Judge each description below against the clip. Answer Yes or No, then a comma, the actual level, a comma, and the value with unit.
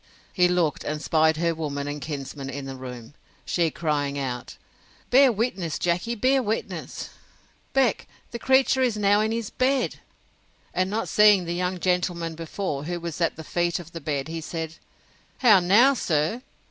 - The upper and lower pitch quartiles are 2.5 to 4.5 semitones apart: No, wide, 5.6 semitones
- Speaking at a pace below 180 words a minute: Yes, average, 170 wpm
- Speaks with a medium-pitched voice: Yes, medium, 170 Hz